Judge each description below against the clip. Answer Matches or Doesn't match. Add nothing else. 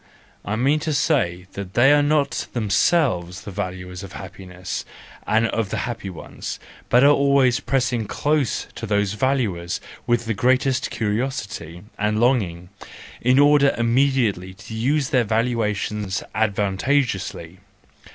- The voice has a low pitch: Matches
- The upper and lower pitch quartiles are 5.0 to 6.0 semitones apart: Matches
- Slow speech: Matches